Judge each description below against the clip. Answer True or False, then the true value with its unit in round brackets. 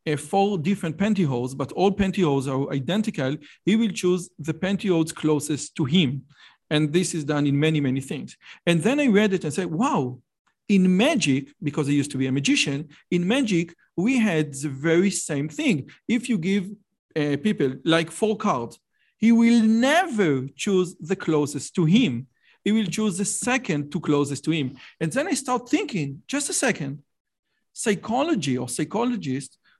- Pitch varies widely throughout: True (6.4 semitones)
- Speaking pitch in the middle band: True (175 Hz)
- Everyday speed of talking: False (175 wpm)